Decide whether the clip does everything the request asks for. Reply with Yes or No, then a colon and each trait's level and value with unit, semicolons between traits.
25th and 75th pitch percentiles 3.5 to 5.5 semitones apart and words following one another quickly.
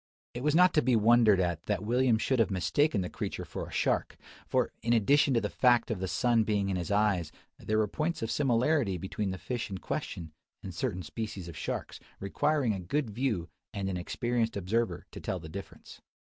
Yes: average, 4.5 semitones; fast, 210 wpm